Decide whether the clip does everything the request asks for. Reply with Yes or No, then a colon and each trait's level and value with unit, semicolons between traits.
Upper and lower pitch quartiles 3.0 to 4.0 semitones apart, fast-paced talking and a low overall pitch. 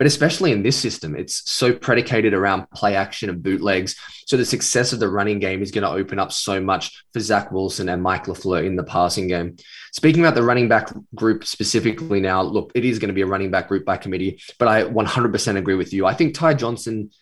Yes: average, 3.3 semitones; fast, 235 wpm; low, 100 Hz